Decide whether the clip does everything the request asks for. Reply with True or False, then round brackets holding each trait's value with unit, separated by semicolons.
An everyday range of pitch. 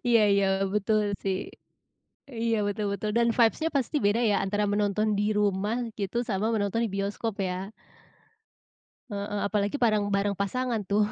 False (2.0 semitones)